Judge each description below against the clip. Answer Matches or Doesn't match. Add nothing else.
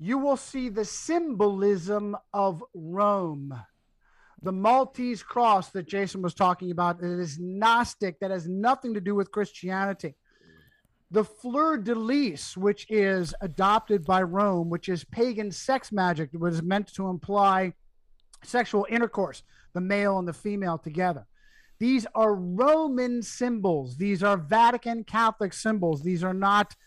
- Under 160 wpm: Matches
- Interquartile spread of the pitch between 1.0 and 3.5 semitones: Doesn't match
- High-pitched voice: Matches